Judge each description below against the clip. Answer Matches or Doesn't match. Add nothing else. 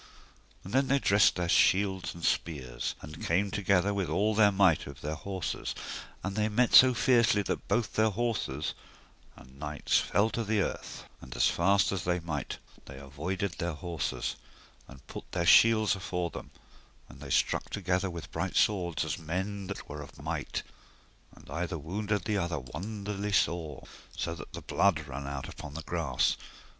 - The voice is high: Doesn't match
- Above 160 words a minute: Matches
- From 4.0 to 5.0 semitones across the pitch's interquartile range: Matches